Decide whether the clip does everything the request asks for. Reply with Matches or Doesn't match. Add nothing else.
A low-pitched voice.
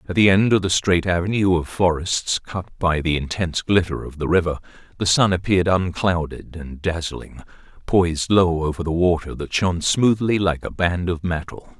Matches